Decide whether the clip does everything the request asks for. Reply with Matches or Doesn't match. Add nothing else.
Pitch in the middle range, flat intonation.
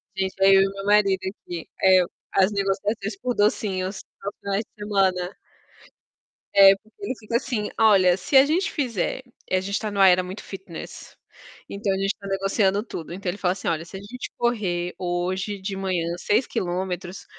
Doesn't match